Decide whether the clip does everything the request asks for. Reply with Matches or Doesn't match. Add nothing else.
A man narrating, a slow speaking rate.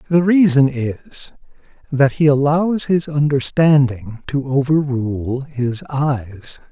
Matches